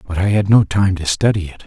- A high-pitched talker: No, very low, 95 Hz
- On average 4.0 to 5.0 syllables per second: No, 6.0 syllables/s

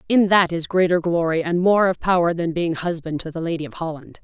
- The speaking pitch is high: No, medium, 170 Hz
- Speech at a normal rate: No, fast, 240 wpm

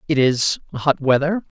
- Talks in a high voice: No, medium, 145 Hz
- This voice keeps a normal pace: Yes, average, 150 wpm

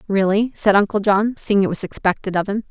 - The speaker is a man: No, female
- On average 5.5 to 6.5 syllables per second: Yes, 5.7 syllables/s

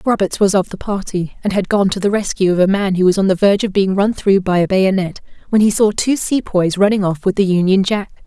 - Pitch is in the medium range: No, high, 195 Hz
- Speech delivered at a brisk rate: Yes, fast, 270 wpm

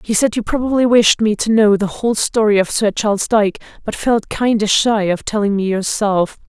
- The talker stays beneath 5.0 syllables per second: No, 5.3 syllables/s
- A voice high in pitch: Yes, high, 215 Hz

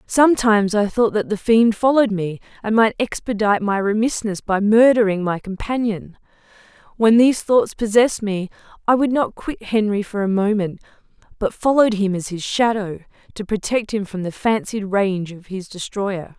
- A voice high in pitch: Yes, high, 210 Hz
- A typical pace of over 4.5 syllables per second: Yes, 5.1 syllables/s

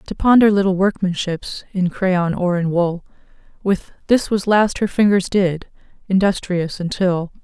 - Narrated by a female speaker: Yes, female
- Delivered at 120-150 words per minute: Yes, average, 145 wpm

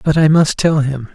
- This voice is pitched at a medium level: Yes, medium, 150 Hz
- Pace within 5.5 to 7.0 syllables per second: No, 4.9 syllables/s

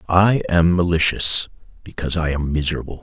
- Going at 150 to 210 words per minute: No, average, 140 wpm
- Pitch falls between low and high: No, very low, 85 Hz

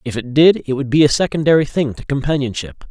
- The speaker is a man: Yes, male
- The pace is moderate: No, fast, 225 wpm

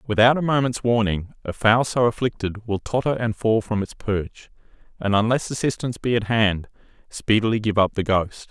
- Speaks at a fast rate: No, average, 185 wpm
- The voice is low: Yes, low, 110 Hz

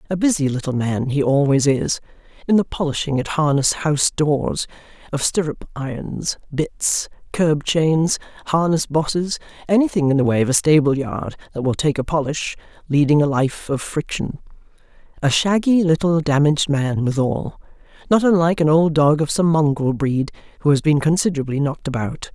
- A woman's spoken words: Yes, female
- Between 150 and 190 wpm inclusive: Yes, average, 165 wpm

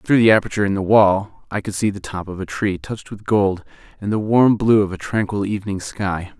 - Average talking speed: No, fast, 245 wpm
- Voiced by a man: Yes, male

